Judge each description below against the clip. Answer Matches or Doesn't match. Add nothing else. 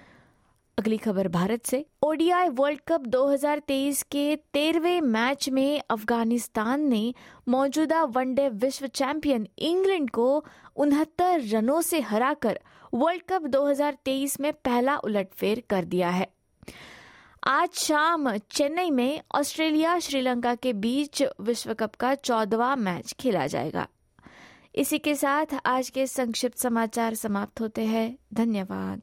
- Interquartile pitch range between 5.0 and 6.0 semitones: Doesn't match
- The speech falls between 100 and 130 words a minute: Matches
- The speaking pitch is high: Matches